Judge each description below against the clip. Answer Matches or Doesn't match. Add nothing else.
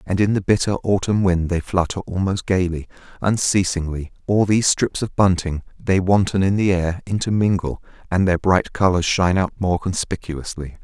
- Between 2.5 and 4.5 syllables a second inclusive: Doesn't match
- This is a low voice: Matches